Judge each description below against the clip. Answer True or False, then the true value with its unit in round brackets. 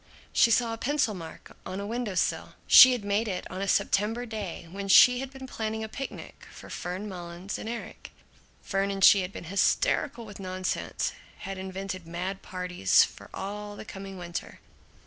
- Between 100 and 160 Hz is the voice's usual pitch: False (200 Hz)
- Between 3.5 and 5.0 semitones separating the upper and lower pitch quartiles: False (3.1 semitones)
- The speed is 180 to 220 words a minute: True (185 wpm)